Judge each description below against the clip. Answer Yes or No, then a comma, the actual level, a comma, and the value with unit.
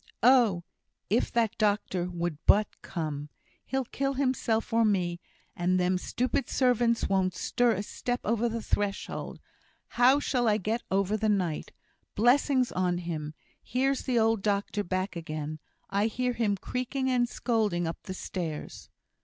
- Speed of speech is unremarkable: Yes, average, 150 wpm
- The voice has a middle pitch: No, high, 210 Hz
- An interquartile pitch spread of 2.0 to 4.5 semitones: No, average, 5.1 semitones